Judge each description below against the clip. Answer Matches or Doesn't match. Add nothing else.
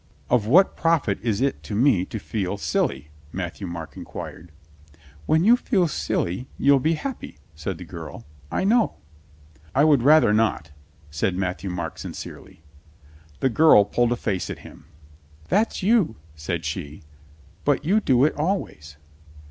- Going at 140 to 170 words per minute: Matches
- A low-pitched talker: Matches